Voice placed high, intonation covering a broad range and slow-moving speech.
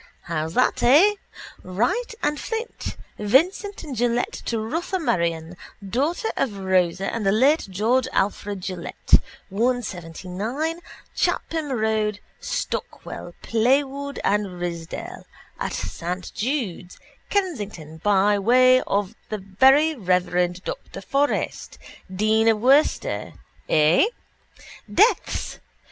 Yes: high, 220 Hz; wide, 7.0 semitones; slow, 100 wpm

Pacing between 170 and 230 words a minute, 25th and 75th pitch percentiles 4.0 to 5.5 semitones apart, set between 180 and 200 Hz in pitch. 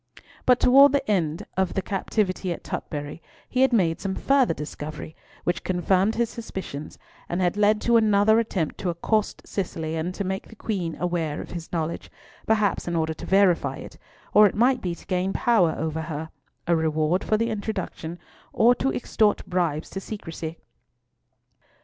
Yes: average, 175 wpm; average, 4.7 semitones; medium, 185 Hz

